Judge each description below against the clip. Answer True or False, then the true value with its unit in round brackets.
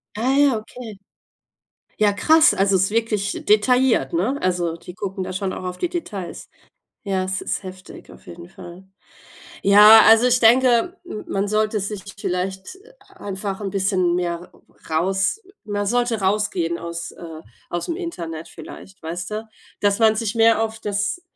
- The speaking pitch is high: True (200 Hz)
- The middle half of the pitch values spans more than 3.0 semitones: True (3.4 semitones)